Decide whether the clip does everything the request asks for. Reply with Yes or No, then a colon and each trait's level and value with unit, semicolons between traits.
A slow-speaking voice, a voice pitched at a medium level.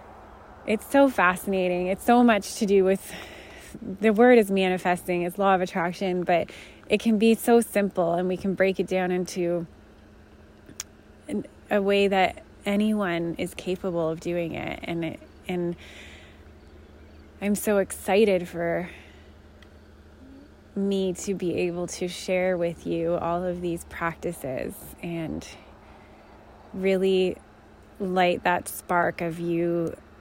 Yes: slow, 130 wpm; medium, 175 Hz